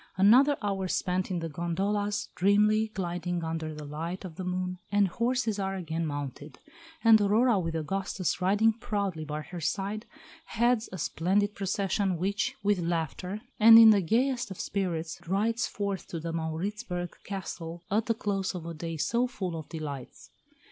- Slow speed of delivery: No, average, 165 wpm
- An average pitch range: Yes, average, 3.8 semitones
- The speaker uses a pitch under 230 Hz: Yes, high, 190 Hz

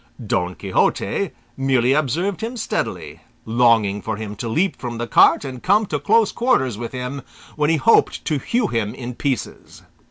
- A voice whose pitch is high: No, low, 130 Hz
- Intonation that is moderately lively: No, wide, 6.2 semitones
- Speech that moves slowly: No, average, 170 wpm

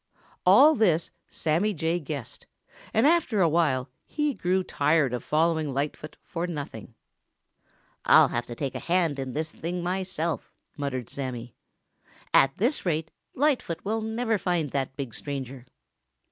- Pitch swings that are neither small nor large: Yes, average, 5.0 semitones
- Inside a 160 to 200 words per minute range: No, average, 145 wpm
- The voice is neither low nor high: Yes, medium, 160 Hz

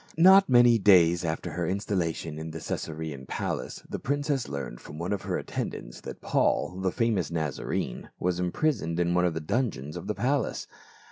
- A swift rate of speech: No, average, 190 wpm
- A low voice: Yes, very low, 90 Hz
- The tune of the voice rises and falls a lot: Yes, wide, 6.2 semitones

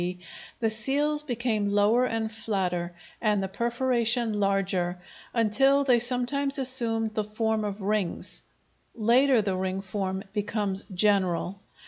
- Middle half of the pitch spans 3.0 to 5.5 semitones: Yes, average, 3.6 semitones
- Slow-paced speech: Yes, slow, 125 wpm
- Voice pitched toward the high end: Yes, high, 215 Hz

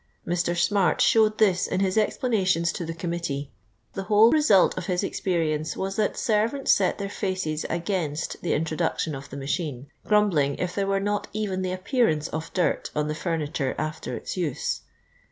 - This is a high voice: No, medium, 180 Hz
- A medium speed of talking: Yes, average, 170 wpm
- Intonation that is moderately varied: Yes, average, 4.4 semitones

